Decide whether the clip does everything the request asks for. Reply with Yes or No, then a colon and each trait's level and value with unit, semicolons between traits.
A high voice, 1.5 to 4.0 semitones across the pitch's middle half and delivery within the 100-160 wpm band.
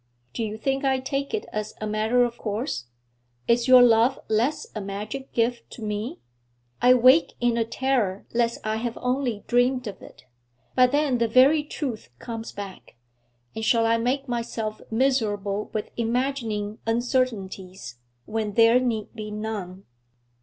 Yes: high, 230 Hz; average, 3.0 semitones; average, 155 wpm